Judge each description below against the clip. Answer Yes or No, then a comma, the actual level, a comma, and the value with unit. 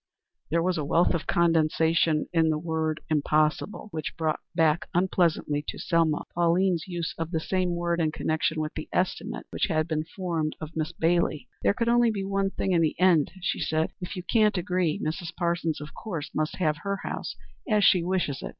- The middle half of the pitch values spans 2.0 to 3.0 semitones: Yes, narrow, 2.6 semitones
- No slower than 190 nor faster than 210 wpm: Yes, fast, 205 wpm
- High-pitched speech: No, medium, 165 Hz